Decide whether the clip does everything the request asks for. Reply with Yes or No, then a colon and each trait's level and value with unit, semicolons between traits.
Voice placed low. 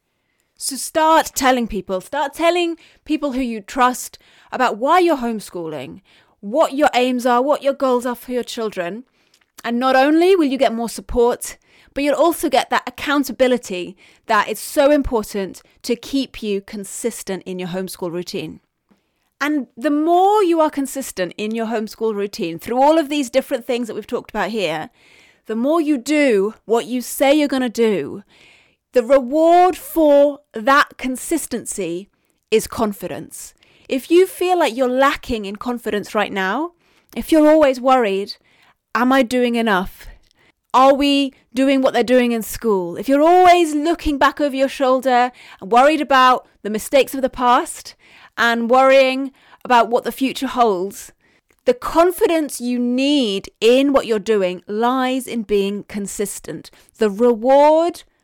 No: very high, 255 Hz